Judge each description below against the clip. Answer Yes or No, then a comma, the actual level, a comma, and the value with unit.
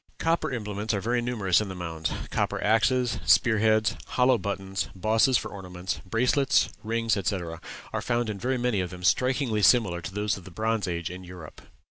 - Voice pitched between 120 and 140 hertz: No, low, 105 Hz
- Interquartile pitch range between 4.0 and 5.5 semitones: Yes, average, 4.3 semitones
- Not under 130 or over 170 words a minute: No, average, 185 wpm